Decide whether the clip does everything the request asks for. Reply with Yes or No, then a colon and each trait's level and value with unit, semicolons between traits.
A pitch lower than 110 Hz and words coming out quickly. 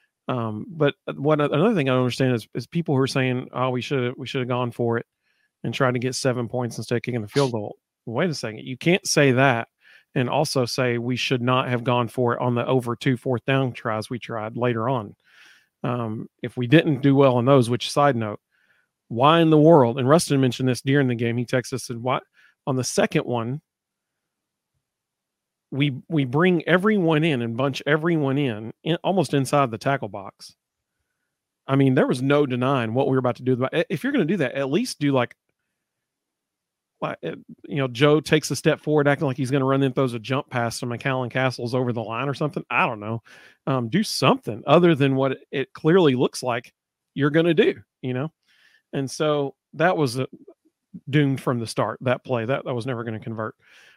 No: low, 130 Hz; fast, 220 wpm